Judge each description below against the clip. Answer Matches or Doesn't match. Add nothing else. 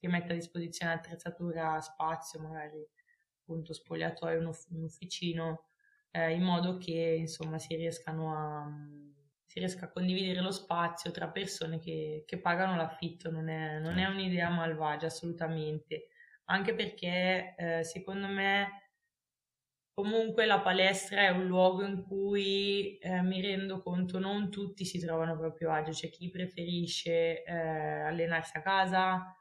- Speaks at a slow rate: Doesn't match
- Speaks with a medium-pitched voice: Matches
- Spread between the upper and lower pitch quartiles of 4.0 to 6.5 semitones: Doesn't match